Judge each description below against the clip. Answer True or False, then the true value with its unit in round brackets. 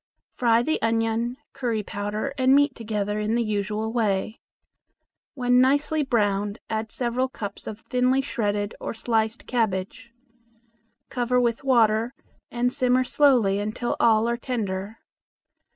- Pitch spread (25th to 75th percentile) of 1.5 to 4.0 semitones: True (2.8 semitones)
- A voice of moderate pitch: False (230 Hz)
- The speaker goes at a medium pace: False (130 wpm)